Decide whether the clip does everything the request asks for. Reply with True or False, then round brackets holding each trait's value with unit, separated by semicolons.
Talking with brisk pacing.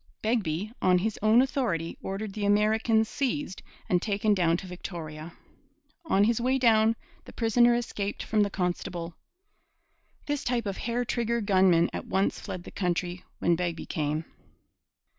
False (150 wpm)